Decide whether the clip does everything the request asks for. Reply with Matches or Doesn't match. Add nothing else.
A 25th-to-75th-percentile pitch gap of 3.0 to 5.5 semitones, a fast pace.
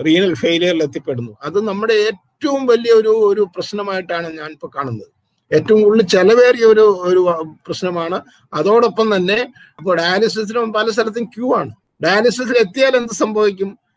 Matches